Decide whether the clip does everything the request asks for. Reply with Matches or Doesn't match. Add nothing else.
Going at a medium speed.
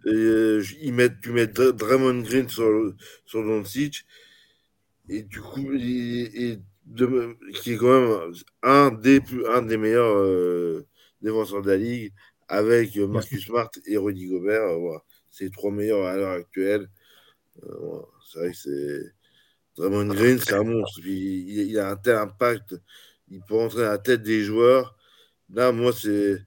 Matches